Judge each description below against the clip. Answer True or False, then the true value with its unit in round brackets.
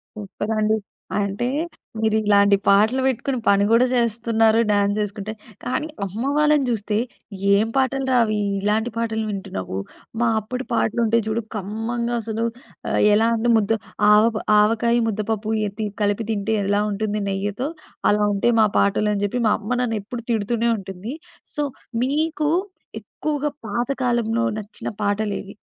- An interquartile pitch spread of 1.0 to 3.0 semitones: True (2.5 semitones)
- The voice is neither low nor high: False (220 Hz)